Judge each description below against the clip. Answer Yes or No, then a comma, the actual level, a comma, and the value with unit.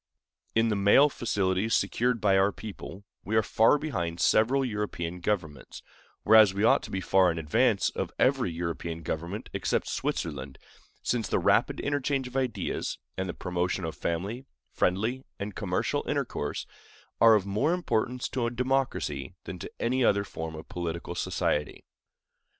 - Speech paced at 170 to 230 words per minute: No, average, 155 wpm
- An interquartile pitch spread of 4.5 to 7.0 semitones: Yes, average, 5.3 semitones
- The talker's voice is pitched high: No, low, 100 Hz